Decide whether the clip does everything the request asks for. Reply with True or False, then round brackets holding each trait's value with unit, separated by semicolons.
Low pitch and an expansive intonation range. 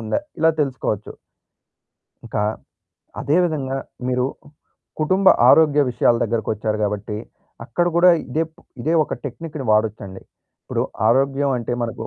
True (130 Hz; 5.9 semitones)